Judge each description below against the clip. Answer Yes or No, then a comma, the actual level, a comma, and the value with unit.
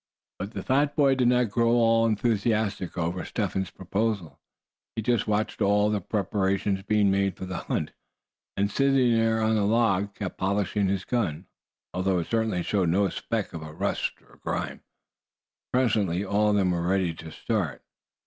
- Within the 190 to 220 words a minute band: No, average, 175 wpm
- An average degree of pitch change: Yes, average, 3.0 semitones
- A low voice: Yes, low, 100 Hz